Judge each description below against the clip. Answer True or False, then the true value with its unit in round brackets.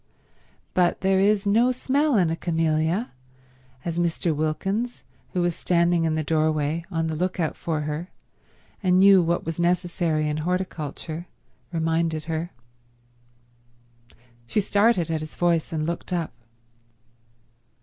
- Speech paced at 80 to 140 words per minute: True (135 wpm)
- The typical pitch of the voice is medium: True (170 Hz)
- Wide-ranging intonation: False (2.7 semitones)